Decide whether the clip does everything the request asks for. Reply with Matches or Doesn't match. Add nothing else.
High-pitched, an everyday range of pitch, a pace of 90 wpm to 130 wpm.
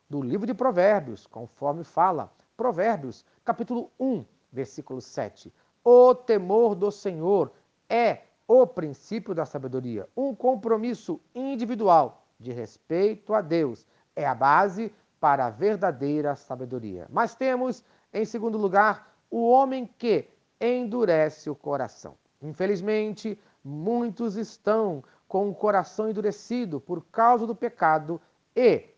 Doesn't match